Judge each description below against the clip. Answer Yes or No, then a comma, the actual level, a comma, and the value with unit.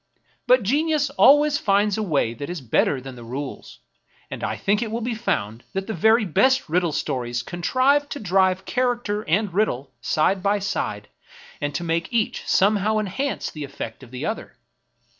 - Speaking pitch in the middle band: No, high, 195 Hz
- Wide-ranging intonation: Yes, wide, 7.9 semitones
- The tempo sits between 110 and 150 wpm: No, average, 180 wpm